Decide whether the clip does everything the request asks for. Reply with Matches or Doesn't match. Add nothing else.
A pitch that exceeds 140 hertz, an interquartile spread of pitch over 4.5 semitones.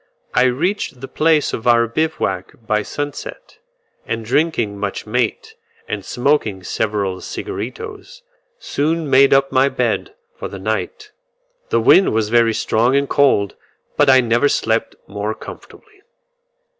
Doesn't match